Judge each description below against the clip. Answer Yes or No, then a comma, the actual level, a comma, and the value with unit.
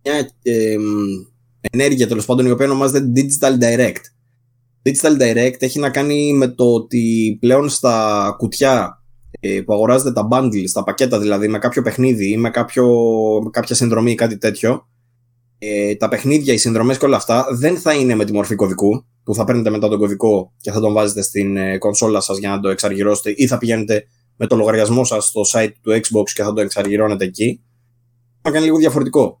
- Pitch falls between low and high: No, low, 115 Hz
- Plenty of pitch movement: No, average, 3.1 semitones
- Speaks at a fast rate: Yes, fast, 190 wpm